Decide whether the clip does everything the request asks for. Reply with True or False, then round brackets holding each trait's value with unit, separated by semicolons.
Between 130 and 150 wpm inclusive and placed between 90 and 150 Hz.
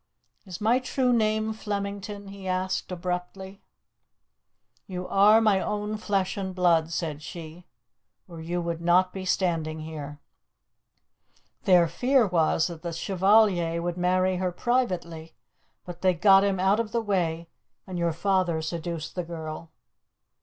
False (140 wpm; 185 Hz)